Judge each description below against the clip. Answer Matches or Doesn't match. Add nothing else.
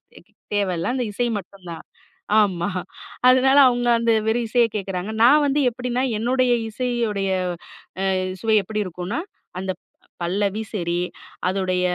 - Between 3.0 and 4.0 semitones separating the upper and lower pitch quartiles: Doesn't match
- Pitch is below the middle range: Doesn't match